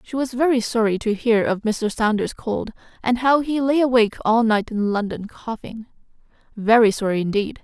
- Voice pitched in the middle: No, high, 230 Hz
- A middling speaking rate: Yes, average, 180 wpm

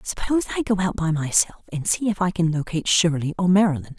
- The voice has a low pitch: No, medium, 180 Hz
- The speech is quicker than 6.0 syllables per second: Yes, 6.4 syllables/s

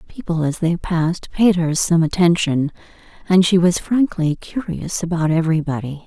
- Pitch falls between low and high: Yes, medium, 170 Hz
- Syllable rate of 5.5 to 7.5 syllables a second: No, 4.9 syllables/s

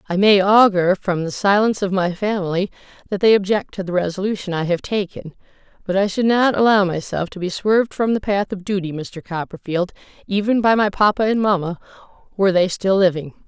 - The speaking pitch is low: No, high, 195 Hz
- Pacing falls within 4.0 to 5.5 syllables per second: No, 5.7 syllables/s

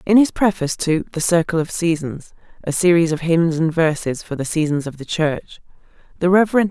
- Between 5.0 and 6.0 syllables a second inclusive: Yes, 5.3 syllables/s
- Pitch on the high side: No, medium, 165 Hz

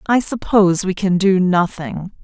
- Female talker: Yes, female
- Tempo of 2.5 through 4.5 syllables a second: Yes, 4.4 syllables/s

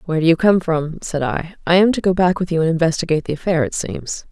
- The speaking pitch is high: No, medium, 170 Hz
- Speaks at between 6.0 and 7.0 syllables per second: Yes, 6.5 syllables/s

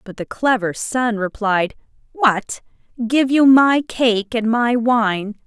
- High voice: Yes, high, 230 Hz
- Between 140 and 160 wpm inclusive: Yes, average, 145 wpm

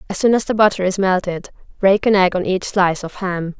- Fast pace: Yes, fast, 250 wpm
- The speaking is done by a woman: Yes, female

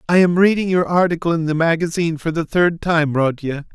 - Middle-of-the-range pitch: Yes, medium, 165 Hz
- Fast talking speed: Yes, fast, 210 wpm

